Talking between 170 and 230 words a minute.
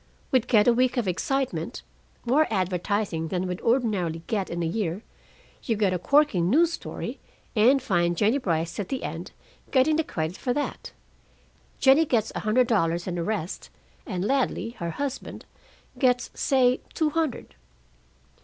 No: average, 160 wpm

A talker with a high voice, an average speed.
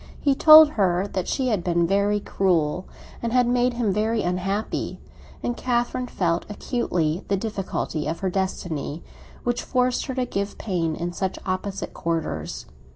Yes: high, 195 Hz; average, 160 wpm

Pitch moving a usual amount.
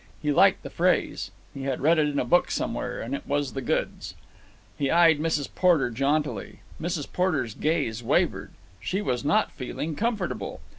Yes: average, 3.6 semitones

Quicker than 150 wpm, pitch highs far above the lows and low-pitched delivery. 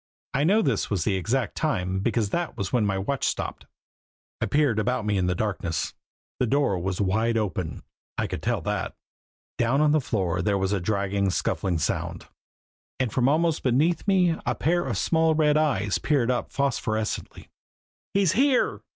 Yes: average, 175 wpm; wide, 7.4 semitones; low, 115 Hz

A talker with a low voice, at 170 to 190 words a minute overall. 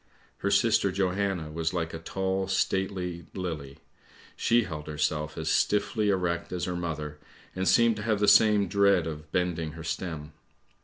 No: very low, 90 Hz; average, 160 wpm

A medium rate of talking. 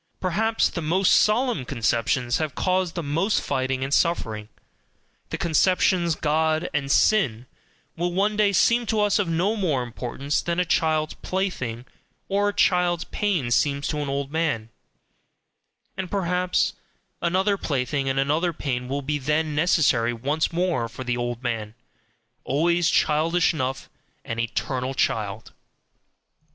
Yes: average, 145 wpm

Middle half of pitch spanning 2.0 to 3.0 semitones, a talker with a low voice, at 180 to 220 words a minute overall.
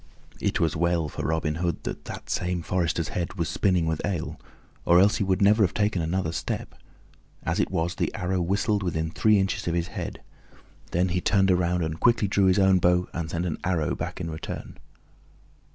Yes: narrow, 2.5 semitones; very low, 90 Hz; average, 200 wpm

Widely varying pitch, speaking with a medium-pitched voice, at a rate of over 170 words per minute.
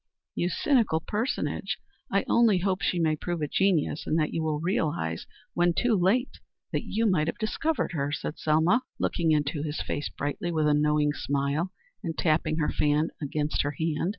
No: average, 3.5 semitones; medium, 160 Hz; average, 180 wpm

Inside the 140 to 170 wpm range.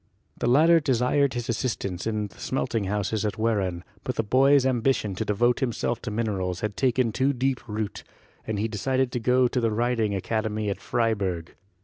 No: average, 185 wpm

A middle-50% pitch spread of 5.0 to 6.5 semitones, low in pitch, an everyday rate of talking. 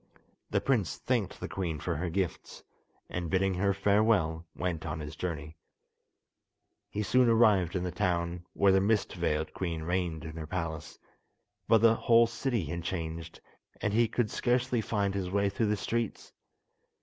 No: average, 4.4 semitones; very low, 95 Hz; average, 165 wpm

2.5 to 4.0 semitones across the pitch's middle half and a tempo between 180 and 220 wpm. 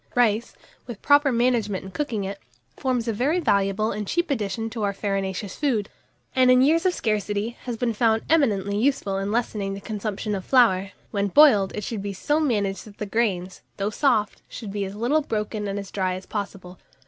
Yes: average, 3.7 semitones; average, 195 wpm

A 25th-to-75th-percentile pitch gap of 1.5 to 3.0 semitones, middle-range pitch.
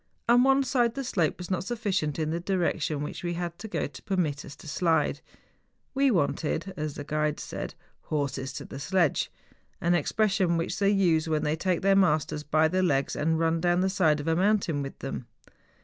No: average, 4.0 semitones; medium, 170 Hz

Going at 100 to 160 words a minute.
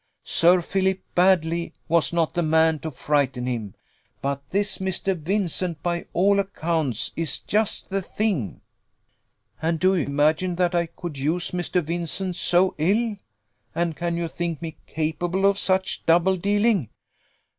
Yes: average, 145 wpm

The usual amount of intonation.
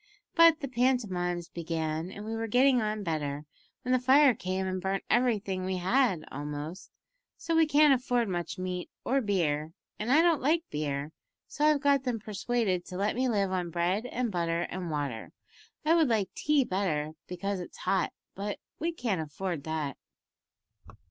No: wide, 6.6 semitones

